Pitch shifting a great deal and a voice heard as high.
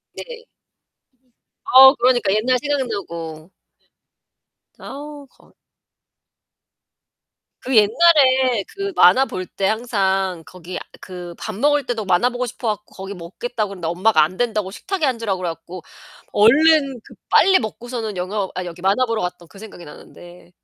Yes: wide, 5.8 semitones; high, 215 Hz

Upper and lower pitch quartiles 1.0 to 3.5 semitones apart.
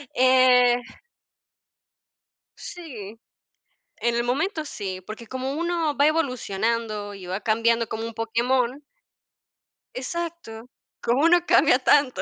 No: average, 4.3 semitones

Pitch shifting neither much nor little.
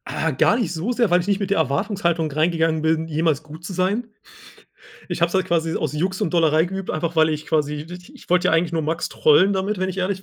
Yes: average, 3.0 semitones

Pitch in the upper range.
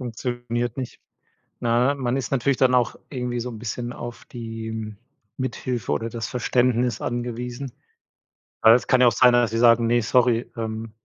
No: low, 120 Hz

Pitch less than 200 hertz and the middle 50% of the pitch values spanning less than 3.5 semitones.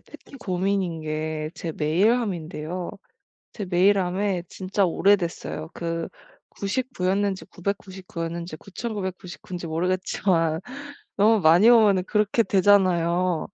Yes: medium, 185 Hz; average, 3.1 semitones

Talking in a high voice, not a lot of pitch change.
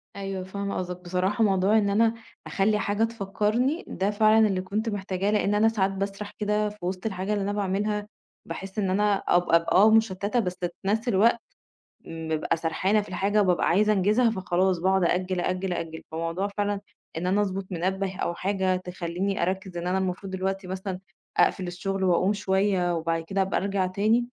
Yes: high, 195 Hz; narrow, 2.1 semitones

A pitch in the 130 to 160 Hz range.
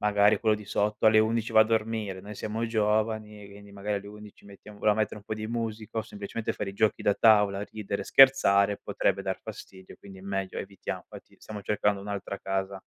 No: low, 105 Hz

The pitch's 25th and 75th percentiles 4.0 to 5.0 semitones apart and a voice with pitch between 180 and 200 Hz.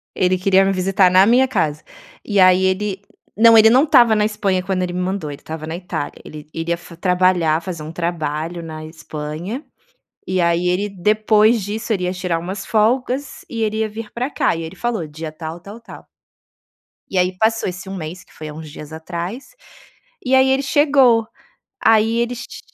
Yes: average, 4.6 semitones; medium, 185 Hz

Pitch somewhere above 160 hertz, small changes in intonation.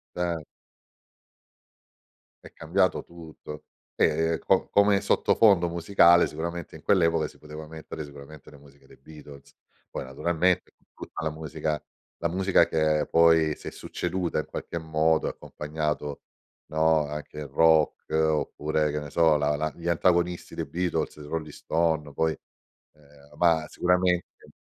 No: very low, 80 Hz; narrow, 2.1 semitones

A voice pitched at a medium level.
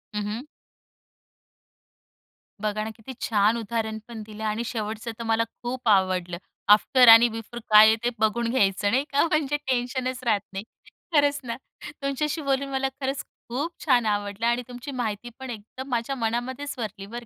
No: high, 235 Hz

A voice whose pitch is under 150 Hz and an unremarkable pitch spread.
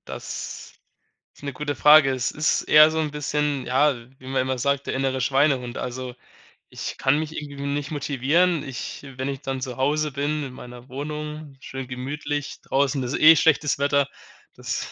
No: medium, 140 Hz; narrow, 2.2 semitones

